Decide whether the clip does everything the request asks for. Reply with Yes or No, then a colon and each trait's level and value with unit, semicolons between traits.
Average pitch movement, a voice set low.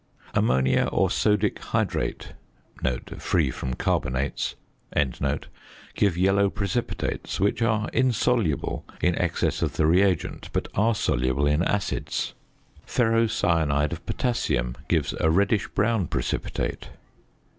No: wide, 6.4 semitones; very low, 95 Hz